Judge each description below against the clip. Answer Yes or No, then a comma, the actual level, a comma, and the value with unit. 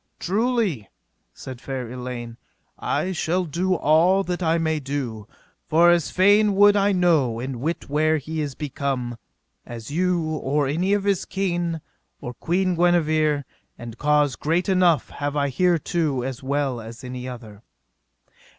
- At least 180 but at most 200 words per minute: No, average, 150 wpm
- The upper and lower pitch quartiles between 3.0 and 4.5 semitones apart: No, average, 5.3 semitones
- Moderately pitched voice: Yes, medium, 155 Hz